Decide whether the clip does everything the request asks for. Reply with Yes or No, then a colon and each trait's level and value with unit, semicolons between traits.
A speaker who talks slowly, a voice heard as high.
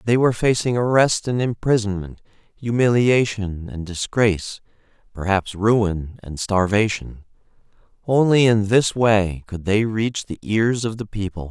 No: slow, 125 wpm; low, 105 Hz